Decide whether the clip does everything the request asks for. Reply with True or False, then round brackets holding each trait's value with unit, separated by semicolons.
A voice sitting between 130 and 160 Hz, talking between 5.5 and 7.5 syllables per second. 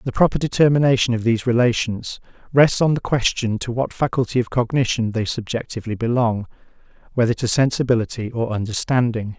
False (120 Hz; 5.9 syllables/s)